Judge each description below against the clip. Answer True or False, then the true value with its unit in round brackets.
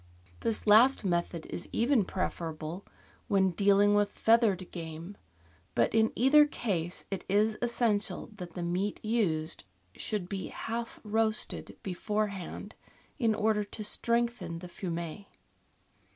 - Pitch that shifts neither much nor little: True (4.0 semitones)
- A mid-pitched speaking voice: False (205 Hz)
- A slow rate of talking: True (125 wpm)